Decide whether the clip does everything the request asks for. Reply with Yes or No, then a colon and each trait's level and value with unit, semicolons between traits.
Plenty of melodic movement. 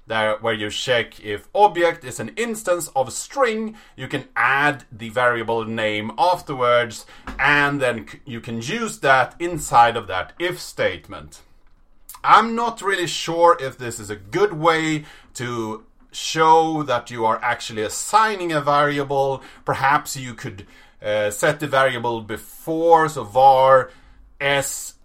Yes: wide, 6.1 semitones